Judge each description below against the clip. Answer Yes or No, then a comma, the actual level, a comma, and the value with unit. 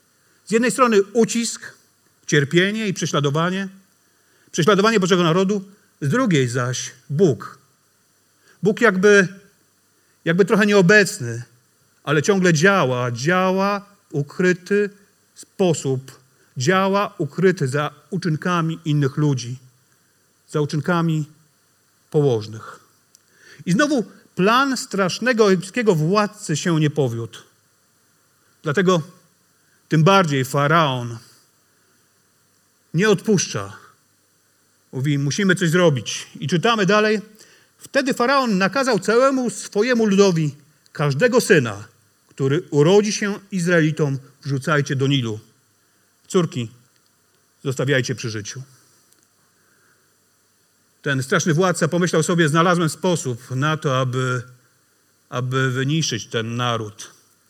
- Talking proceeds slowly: Yes, slow, 95 wpm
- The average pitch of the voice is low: No, medium, 160 Hz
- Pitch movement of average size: No, wide, 6.5 semitones